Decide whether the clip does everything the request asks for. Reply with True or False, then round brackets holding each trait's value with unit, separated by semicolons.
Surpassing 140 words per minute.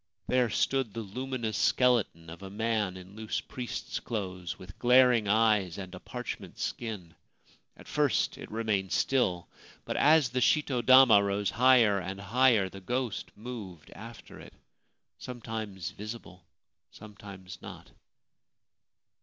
False (135 wpm)